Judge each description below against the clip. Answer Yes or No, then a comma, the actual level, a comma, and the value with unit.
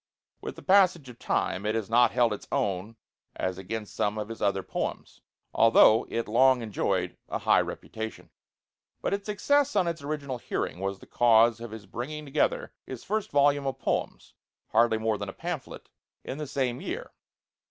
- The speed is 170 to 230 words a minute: Yes, average, 180 wpm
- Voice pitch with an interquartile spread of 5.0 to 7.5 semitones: Yes, average, 5.3 semitones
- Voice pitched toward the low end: Yes, low, 120 Hz